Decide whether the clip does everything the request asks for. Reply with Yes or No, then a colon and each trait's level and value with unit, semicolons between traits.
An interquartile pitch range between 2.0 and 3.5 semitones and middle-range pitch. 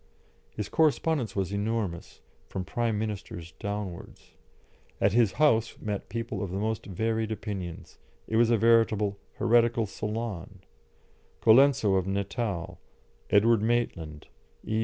No: average, 2.9 semitones; low, 110 Hz